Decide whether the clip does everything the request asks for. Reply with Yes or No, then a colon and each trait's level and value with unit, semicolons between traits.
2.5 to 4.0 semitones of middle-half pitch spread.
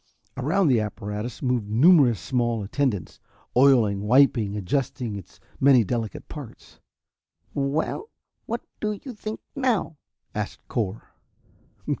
No: wide, 5.6 semitones